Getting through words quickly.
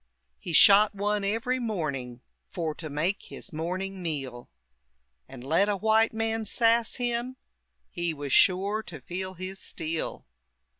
No: average, 140 wpm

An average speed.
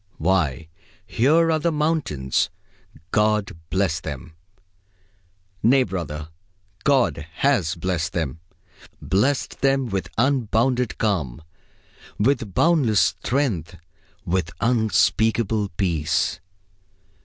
No: slow, 85 wpm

